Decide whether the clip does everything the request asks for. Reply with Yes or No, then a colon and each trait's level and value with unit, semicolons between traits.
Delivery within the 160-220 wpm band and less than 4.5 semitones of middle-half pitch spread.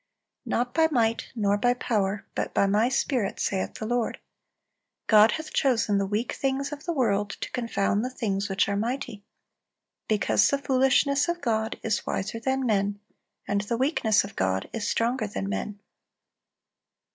Yes: average, 165 wpm; average, 4.0 semitones